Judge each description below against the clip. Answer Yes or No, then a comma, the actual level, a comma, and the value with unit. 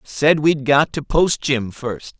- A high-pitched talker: No, medium, 140 Hz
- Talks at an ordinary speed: Yes, average, 190 wpm